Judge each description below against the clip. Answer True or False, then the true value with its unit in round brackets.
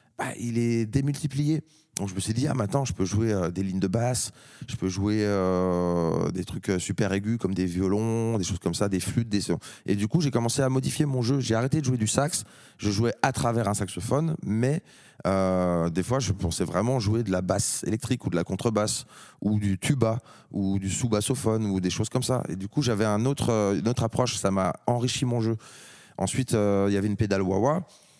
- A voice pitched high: False (110 Hz)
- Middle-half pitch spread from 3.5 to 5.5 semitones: True (4.8 semitones)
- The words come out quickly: True (230 wpm)